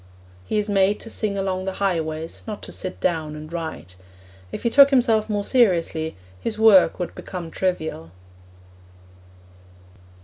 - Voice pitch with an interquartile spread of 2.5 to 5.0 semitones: Yes, average, 4.6 semitones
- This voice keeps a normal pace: Yes, average, 145 wpm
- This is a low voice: No, high, 190 Hz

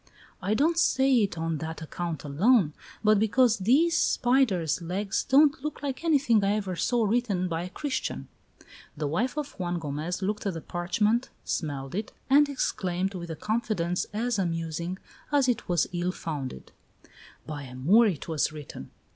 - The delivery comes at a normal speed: Yes, average, 165 wpm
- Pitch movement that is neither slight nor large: No, wide, 6.6 semitones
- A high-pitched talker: Yes, high, 195 Hz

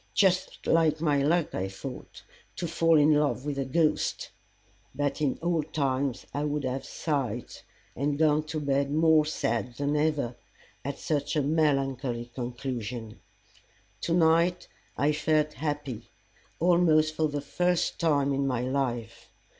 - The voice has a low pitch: No, medium, 145 Hz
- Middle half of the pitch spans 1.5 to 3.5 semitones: Yes, average, 2.7 semitones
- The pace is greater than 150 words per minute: No, average, 145 wpm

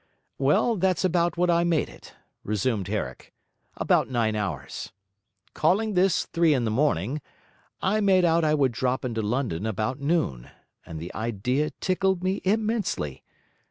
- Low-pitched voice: No, medium, 145 Hz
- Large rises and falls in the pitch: Yes, wide, 8.4 semitones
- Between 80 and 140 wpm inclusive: No, average, 150 wpm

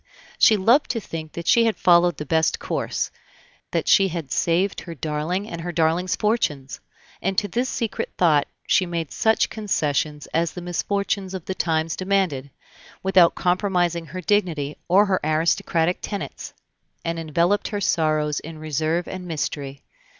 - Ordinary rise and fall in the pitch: Yes, average, 3.4 semitones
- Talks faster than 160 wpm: No, average, 155 wpm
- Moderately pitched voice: Yes, medium, 170 Hz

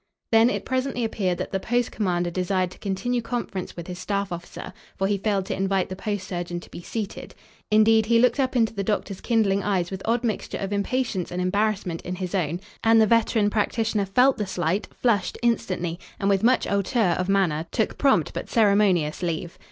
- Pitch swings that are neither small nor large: Yes, average, 3.5 semitones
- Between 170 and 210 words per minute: Yes, average, 200 wpm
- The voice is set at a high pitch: Yes, high, 200 Hz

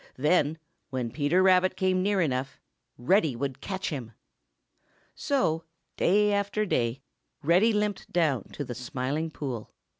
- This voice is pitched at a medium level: Yes, medium, 160 Hz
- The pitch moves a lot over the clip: Yes, wide, 6.4 semitones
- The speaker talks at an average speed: No, slow, 130 wpm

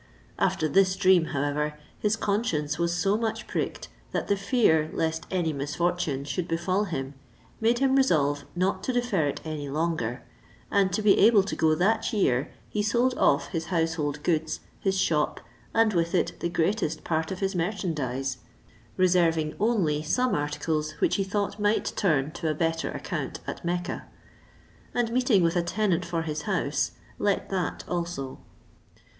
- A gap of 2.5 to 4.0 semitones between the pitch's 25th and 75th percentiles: No, average, 4.6 semitones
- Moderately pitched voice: Yes, medium, 170 Hz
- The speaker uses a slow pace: No, average, 160 wpm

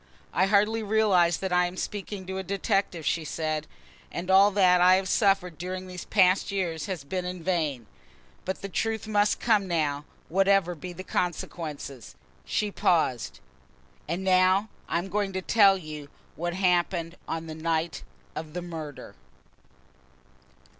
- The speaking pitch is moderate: Yes, medium, 180 Hz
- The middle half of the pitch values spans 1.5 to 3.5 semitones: Yes, average, 3.0 semitones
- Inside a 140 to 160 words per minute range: Yes, average, 155 wpm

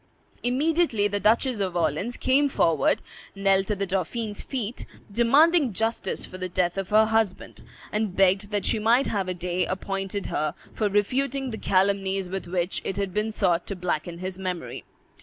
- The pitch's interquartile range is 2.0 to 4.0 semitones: Yes, average, 3.4 semitones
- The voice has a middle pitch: No, high, 200 Hz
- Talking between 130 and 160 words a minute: No, average, 175 wpm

